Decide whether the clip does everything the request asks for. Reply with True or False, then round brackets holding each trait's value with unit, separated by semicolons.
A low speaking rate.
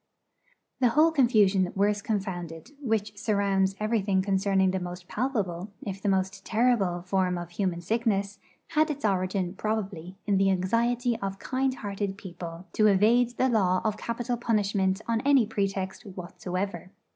False (145 wpm)